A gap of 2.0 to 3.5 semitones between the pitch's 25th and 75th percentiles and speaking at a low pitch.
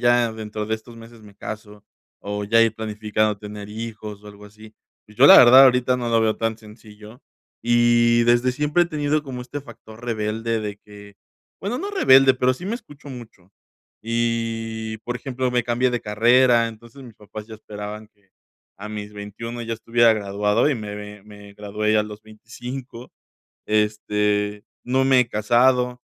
Yes: narrow, 2.5 semitones; low, 115 Hz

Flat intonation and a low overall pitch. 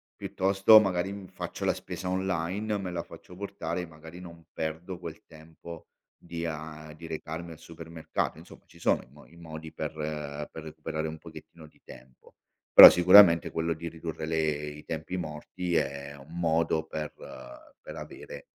Yes: narrow, 2.0 semitones; very low, 80 Hz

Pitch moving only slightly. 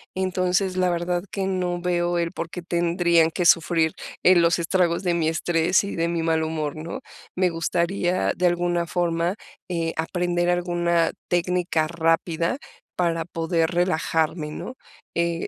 Yes: narrow, 1.2 semitones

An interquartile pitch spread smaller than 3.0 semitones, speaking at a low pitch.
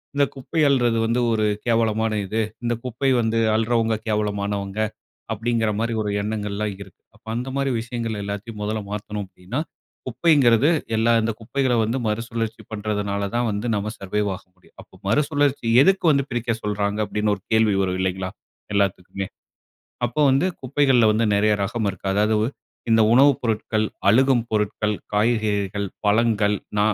Yes: narrow, 2.6 semitones; low, 110 Hz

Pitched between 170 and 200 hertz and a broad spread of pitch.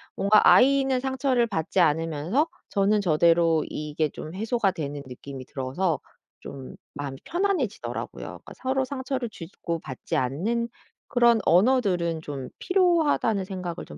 Yes: high, 190 Hz; wide, 8.5 semitones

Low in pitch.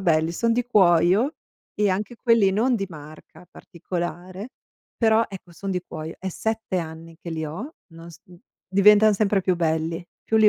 No: medium, 185 Hz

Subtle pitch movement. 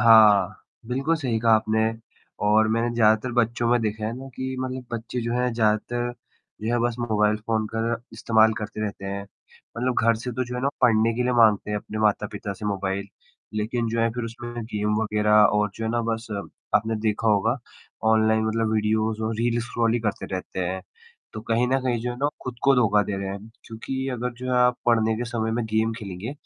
Yes: narrow, 2.1 semitones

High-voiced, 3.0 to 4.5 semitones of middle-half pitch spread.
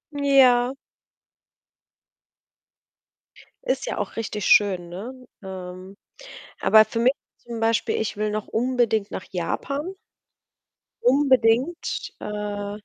Yes: high, 225 Hz; average, 3.7 semitones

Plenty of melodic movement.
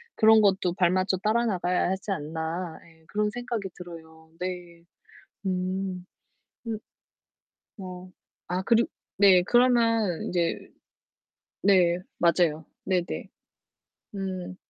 No: narrow, 2.6 semitones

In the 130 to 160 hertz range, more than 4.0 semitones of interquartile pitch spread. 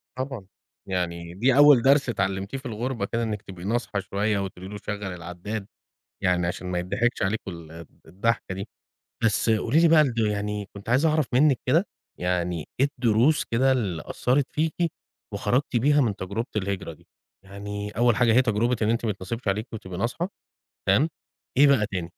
No: low, 105 Hz; average, 4.7 semitones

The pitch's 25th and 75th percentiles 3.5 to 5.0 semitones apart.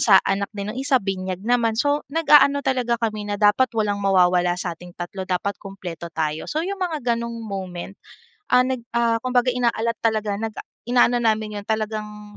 Yes: average, 3.9 semitones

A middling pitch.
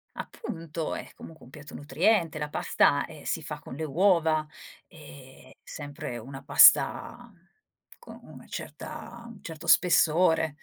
Yes: medium, 160 Hz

